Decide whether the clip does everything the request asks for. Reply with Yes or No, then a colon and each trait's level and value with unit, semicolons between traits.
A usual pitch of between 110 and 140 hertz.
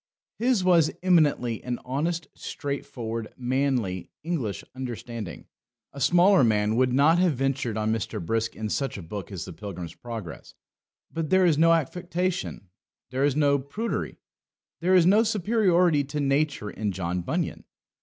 Yes: low, 135 Hz